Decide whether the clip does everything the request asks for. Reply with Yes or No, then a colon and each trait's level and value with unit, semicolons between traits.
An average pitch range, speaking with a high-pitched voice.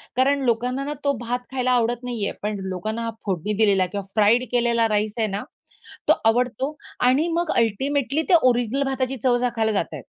Yes: average, 3.3 semitones; high, 240 Hz